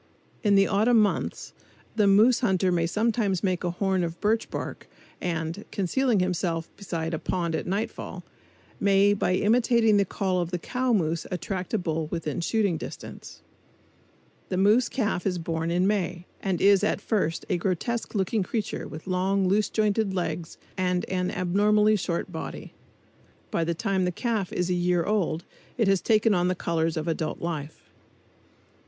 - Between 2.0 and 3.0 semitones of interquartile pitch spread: No, average, 3.4 semitones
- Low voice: No, medium, 185 Hz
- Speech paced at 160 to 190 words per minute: Yes, average, 170 wpm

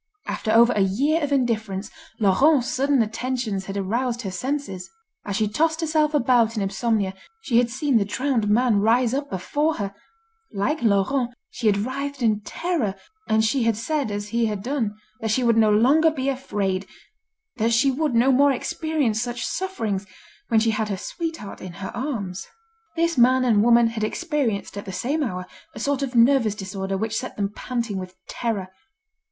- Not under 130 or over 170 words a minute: No, average, 180 wpm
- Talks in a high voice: Yes, high, 235 Hz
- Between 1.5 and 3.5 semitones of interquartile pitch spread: No, average, 4.7 semitones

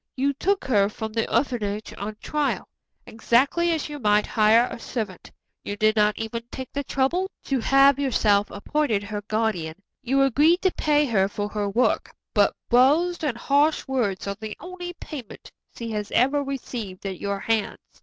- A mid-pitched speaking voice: No, high, 235 Hz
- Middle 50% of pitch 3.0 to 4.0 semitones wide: No, average, 5.2 semitones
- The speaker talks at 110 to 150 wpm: No, average, 175 wpm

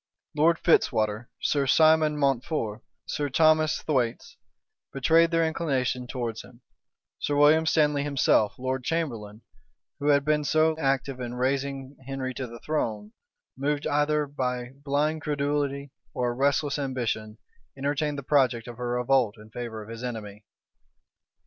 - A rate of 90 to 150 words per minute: Yes, average, 140 wpm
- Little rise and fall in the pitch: No, average, 3.4 semitones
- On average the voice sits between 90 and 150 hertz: Yes, low, 135 Hz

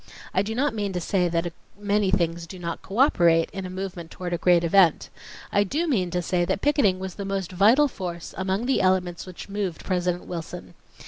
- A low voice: No, medium, 185 Hz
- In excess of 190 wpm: Yes, fast, 205 wpm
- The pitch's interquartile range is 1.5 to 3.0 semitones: Yes, narrow, 2.6 semitones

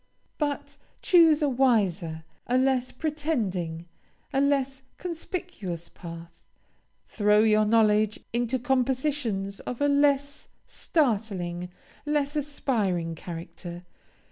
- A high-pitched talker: Yes, high, 240 Hz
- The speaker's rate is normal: No, slow, 95 wpm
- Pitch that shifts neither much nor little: No, wide, 6.8 semitones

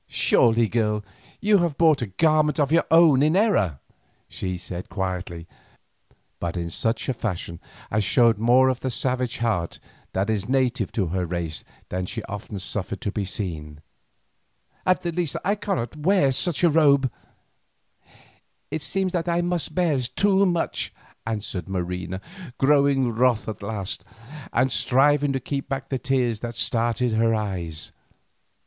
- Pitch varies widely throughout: Yes, wide, 7.0 semitones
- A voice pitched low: Yes, low, 120 Hz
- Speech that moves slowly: No, average, 155 wpm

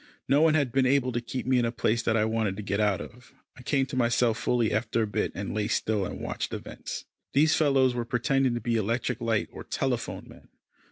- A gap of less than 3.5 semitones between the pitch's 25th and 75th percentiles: Yes, average, 2.9 semitones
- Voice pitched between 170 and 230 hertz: No, low, 120 Hz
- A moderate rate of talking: No, fast, 235 wpm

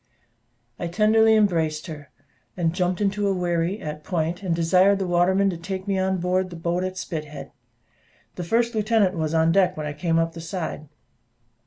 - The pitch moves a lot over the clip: No, average, 2.9 semitones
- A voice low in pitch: No, medium, 180 Hz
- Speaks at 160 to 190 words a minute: Yes, average, 180 wpm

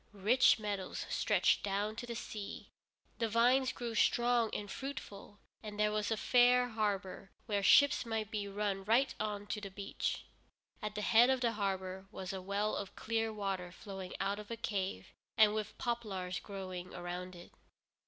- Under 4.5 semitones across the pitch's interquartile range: Yes, average, 2.8 semitones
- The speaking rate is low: No, average, 175 wpm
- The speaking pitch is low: No, high, 210 Hz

